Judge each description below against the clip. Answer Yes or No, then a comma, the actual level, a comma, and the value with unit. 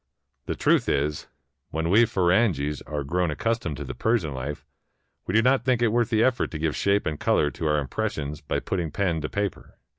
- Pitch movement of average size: No, wide, 6.8 semitones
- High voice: No, very low, 85 Hz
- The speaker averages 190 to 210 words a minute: Yes, fast, 205 wpm